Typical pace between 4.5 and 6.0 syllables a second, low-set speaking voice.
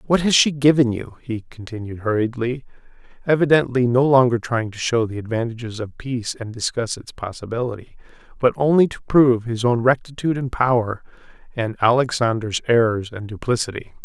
Yes: 5.6 syllables/s; low, 120 Hz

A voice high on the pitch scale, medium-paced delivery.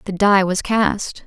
Yes: high, 195 Hz; average, 190 wpm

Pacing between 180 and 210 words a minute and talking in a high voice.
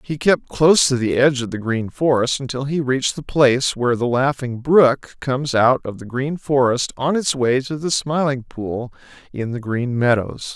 No: fast, 205 wpm; low, 130 Hz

